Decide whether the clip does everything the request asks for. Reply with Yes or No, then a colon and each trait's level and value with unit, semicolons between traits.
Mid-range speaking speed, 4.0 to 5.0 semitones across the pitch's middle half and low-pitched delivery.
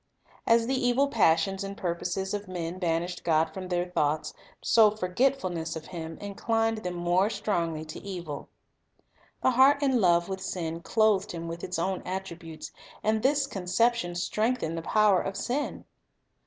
No: average, 160 wpm; average, 4.3 semitones; medium, 185 Hz